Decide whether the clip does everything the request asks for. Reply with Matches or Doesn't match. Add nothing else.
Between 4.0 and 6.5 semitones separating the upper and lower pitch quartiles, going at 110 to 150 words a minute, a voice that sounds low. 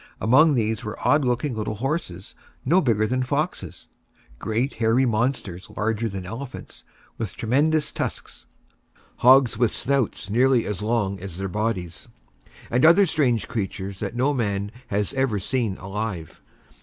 Matches